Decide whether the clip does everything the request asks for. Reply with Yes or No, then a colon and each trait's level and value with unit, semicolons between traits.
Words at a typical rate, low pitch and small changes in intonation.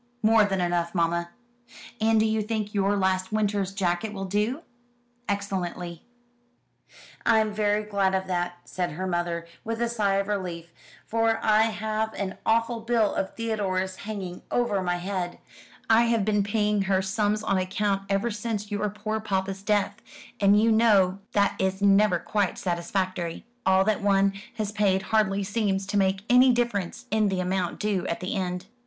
No: average, 165 wpm; high, 200 Hz; narrow, 2.3 semitones